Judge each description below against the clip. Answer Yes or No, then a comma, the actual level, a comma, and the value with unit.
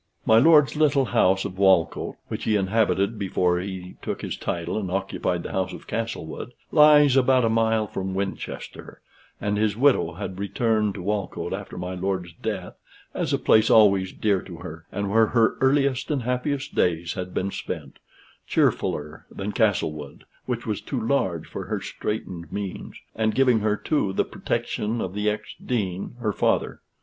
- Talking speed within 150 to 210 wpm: Yes, average, 170 wpm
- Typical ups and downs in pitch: Yes, average, 3.6 semitones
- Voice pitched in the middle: No, low, 105 Hz